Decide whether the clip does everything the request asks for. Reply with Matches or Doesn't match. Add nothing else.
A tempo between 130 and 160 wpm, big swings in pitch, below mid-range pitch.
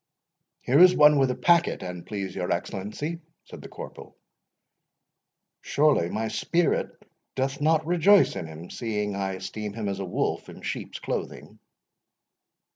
Matches